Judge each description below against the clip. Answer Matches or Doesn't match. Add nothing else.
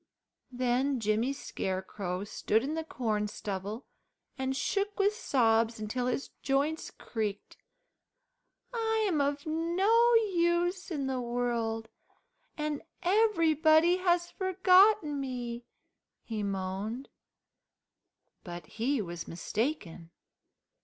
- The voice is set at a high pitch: Matches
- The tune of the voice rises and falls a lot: Matches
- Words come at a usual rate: Doesn't match